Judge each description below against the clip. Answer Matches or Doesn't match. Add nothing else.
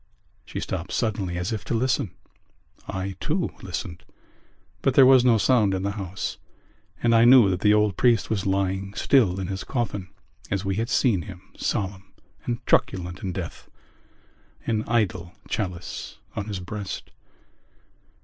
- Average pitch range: Matches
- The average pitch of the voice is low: Matches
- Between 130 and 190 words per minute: Matches